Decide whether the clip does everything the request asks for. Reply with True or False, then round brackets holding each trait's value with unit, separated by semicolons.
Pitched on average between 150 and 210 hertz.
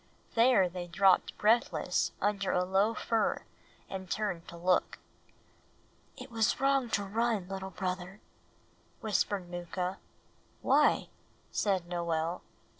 True (190 Hz)